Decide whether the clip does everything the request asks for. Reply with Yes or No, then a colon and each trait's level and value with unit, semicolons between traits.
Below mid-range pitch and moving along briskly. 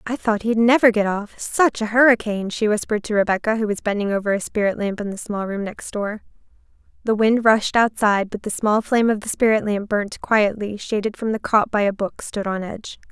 No: high, 215 Hz; fast, 225 wpm